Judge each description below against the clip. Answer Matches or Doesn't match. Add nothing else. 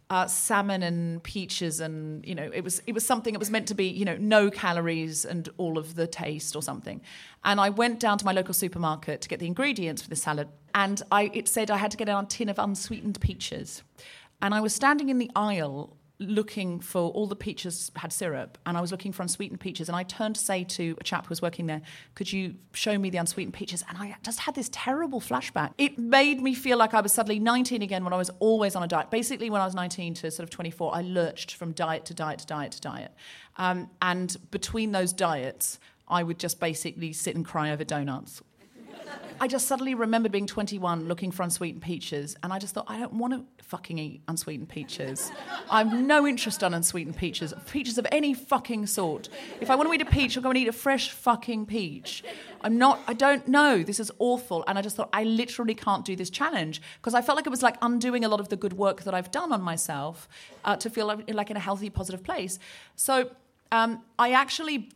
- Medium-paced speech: Doesn't match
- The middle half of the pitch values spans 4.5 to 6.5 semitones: Matches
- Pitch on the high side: Matches